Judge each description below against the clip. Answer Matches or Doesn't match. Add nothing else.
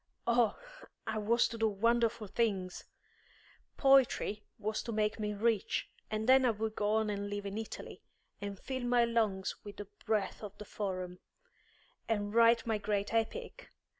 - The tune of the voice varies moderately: Doesn't match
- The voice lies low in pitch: Doesn't match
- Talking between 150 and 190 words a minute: Matches